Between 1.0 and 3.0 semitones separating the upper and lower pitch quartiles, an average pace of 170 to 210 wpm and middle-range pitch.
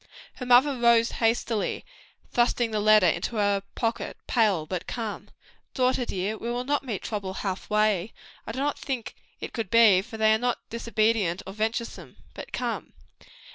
No: narrow, 2.6 semitones; average, 175 wpm; high, 225 Hz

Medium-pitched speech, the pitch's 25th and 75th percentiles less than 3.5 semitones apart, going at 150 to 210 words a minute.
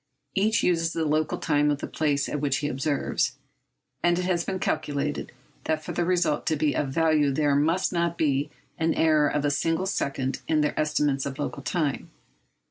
Yes: medium, 150 Hz; narrow, 2.4 semitones; average, 195 wpm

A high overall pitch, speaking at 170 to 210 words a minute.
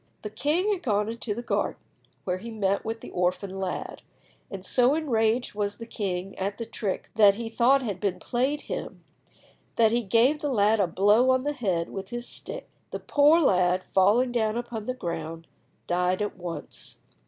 Yes: high, 220 Hz; average, 190 wpm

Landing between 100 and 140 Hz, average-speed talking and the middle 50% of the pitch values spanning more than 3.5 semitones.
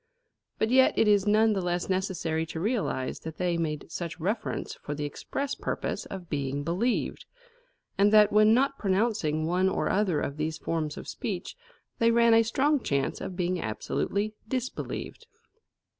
No: high, 190 Hz; average, 165 wpm; average, 5.3 semitones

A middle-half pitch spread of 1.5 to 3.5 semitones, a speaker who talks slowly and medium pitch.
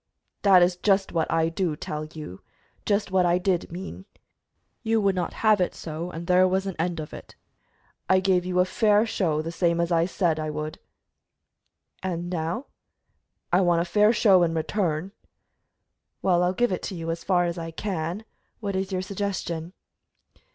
No: narrow, 2.6 semitones; average, 185 wpm; medium, 180 Hz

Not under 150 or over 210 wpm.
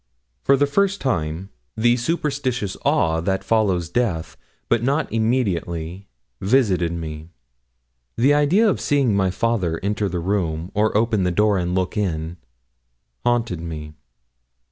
No: slow, 135 wpm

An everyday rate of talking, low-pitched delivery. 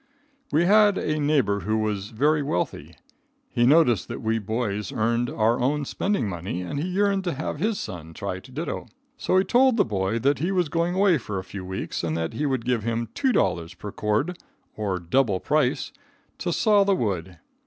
Yes: average, 195 wpm; low, 120 Hz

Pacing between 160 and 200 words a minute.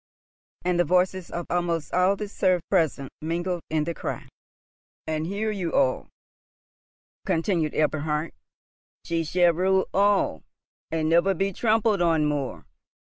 No: slow, 135 wpm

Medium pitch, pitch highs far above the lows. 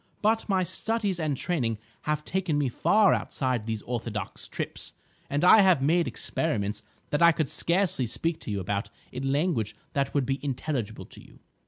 Yes: medium, 145 Hz; wide, 6.4 semitones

